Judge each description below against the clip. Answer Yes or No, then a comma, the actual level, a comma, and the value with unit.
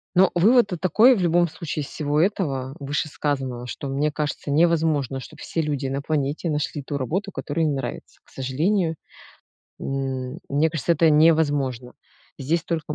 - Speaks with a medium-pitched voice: Yes, medium, 150 Hz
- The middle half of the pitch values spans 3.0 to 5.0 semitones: Yes, average, 3.4 semitones